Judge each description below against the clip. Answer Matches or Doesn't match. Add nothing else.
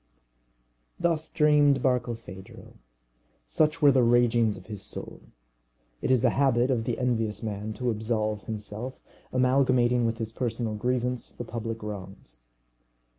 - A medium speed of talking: Doesn't match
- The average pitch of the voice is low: Matches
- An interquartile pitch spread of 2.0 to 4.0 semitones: Matches